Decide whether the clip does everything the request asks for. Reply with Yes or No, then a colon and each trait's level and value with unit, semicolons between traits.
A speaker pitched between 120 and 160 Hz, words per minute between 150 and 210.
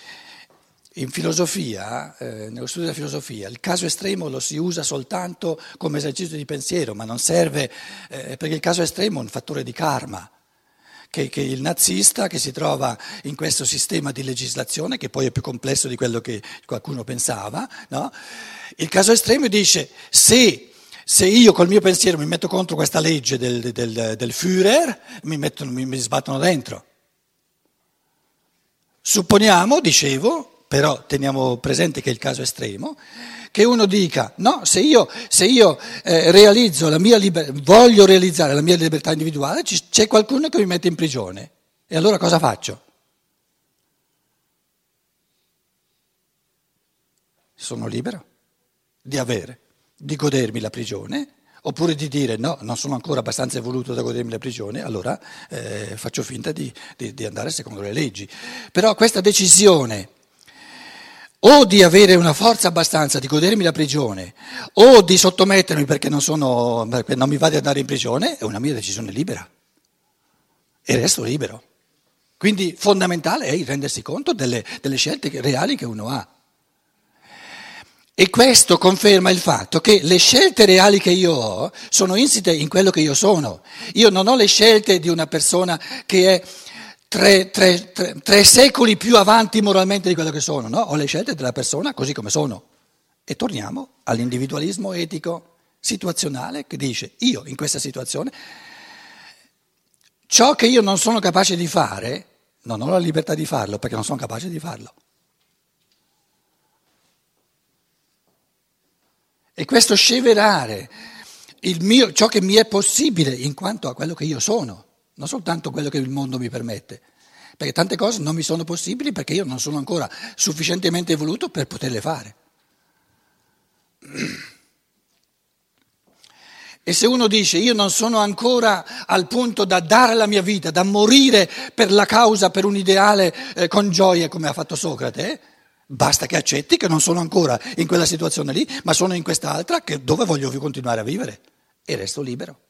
No: medium, 170 Hz; average, 160 wpm